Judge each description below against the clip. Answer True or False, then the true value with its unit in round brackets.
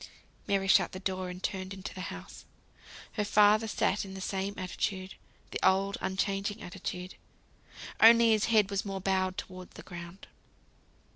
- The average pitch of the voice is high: True (195 Hz)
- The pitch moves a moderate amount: False (1.3 semitones)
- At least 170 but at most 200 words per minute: False (155 wpm)